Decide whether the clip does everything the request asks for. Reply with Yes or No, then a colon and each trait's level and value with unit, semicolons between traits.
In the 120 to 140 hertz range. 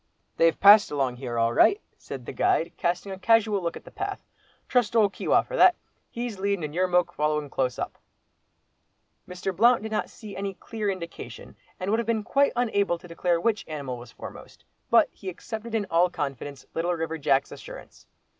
No: medium, 185 Hz